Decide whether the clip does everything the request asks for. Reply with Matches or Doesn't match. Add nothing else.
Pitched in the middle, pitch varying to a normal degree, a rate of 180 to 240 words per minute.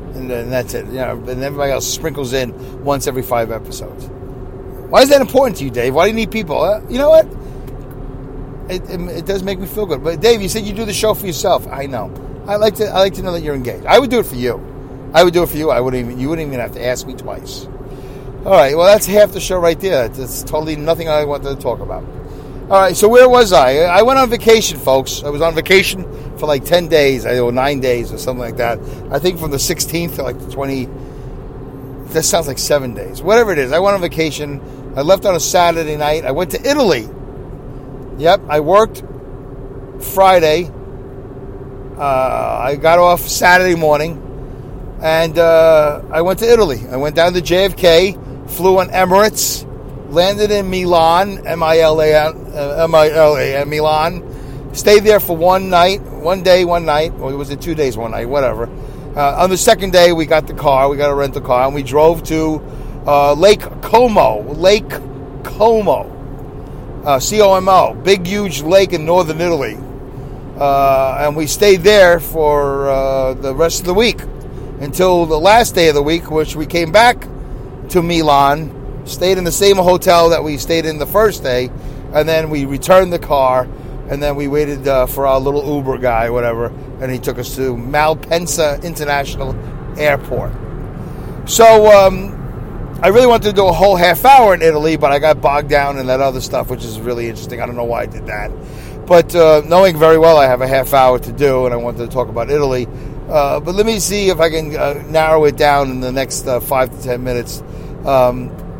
Matches